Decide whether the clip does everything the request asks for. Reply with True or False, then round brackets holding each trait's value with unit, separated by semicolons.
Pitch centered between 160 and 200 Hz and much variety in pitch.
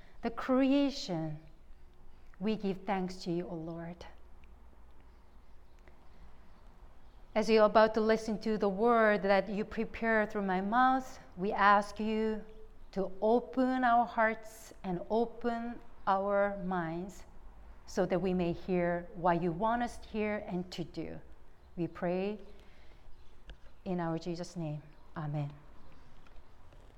True (185 Hz; 6.0 semitones)